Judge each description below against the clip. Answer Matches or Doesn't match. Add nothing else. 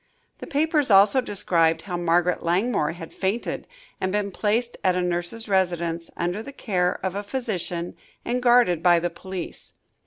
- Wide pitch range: Doesn't match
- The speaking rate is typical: Matches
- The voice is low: Doesn't match